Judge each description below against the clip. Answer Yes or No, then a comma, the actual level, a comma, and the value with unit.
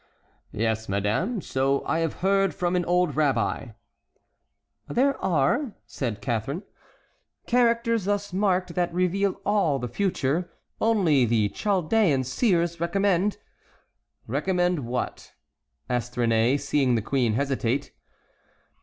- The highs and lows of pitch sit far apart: Yes, wide, 7.3 semitones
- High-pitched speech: No, medium, 170 Hz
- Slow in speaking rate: Yes, slow, 110 wpm